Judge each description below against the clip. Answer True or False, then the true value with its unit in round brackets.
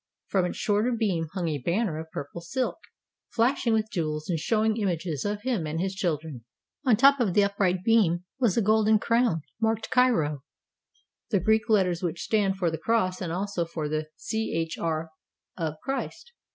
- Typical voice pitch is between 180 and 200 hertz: True (190 Hz)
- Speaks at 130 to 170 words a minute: False (180 wpm)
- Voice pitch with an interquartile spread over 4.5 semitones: True (5.2 semitones)